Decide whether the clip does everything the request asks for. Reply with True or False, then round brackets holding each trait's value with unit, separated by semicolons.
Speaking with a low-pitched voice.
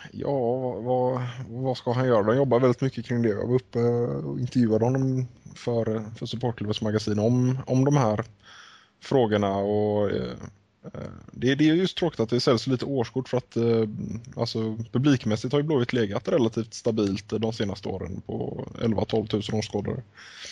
True (120 Hz)